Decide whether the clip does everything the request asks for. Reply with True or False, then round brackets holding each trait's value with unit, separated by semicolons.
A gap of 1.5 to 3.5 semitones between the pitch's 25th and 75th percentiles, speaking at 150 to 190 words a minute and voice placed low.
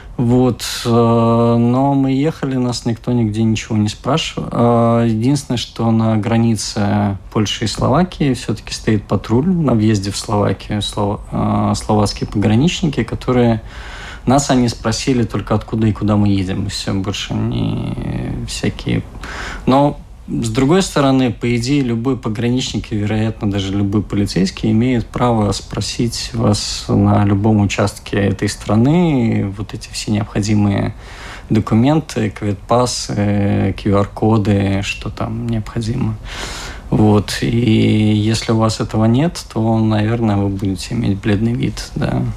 False (2.7 semitones; 125 wpm; 110 Hz)